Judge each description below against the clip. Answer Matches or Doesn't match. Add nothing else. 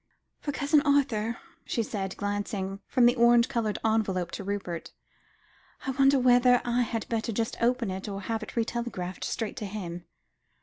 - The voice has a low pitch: Doesn't match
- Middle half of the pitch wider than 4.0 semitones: Doesn't match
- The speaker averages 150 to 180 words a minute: Matches